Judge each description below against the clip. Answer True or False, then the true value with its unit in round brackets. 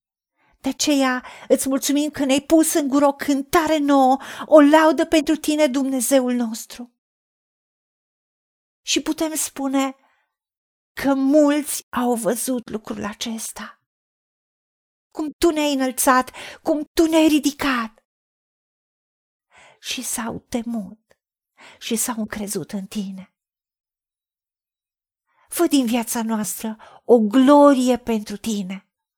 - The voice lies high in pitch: True (260 Hz)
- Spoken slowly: True (105 wpm)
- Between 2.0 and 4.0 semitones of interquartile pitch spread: False (4.7 semitones)